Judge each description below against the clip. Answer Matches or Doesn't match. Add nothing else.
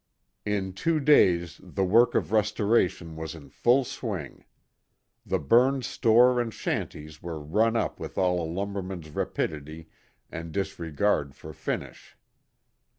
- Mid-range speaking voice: Doesn't match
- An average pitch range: Doesn't match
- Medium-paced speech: Doesn't match